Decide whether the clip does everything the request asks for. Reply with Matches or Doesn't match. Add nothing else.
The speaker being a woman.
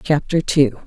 Matches